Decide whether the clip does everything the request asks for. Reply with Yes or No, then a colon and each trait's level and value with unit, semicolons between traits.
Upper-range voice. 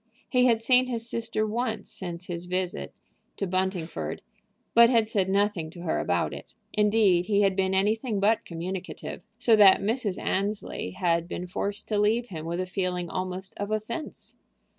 Yes: high, 200 Hz